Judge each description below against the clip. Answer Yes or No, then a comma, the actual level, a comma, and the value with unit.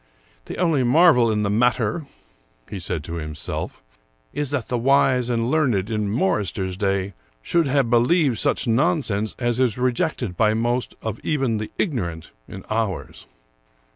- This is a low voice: Yes, low, 115 Hz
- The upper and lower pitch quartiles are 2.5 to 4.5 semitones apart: No, average, 4.9 semitones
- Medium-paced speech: Yes, average, 160 wpm